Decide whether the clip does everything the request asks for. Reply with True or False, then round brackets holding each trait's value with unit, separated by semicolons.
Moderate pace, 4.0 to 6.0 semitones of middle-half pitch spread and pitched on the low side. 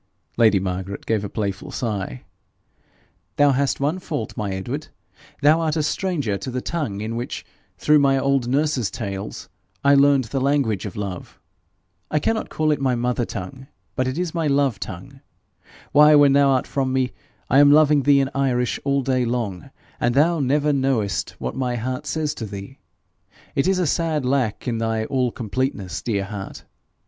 True (180 wpm; 4.6 semitones; 130 Hz)